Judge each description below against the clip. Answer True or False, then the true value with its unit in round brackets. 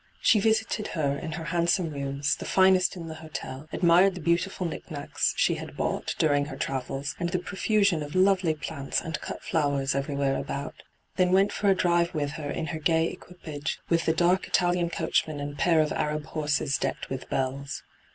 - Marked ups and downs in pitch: False (3.7 semitones)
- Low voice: False (160 Hz)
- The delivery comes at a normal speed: True (190 wpm)